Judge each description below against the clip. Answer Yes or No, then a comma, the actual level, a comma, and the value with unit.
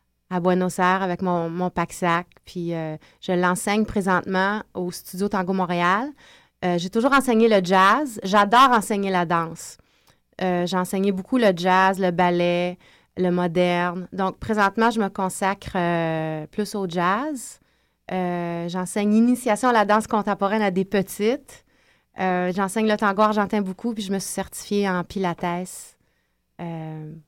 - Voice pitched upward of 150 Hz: Yes, medium, 185 Hz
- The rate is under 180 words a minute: Yes, average, 150 wpm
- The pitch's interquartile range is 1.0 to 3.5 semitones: Yes, narrow, 2.6 semitones